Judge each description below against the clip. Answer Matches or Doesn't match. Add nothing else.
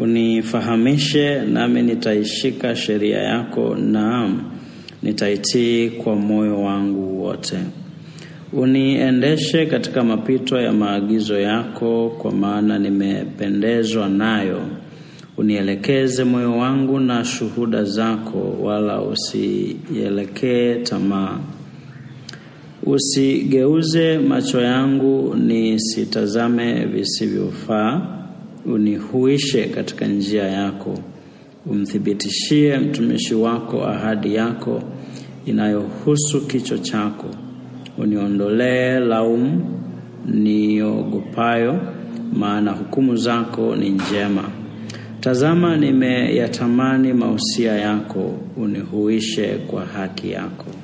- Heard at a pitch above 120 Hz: Doesn't match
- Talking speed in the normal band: Doesn't match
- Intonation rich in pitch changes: Doesn't match